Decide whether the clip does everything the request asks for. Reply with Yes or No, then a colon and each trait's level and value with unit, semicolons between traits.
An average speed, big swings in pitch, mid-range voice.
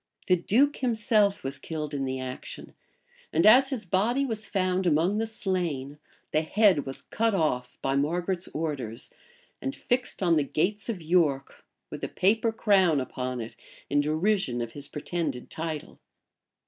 Yes: average, 160 wpm; wide, 6.6 semitones; medium, 170 Hz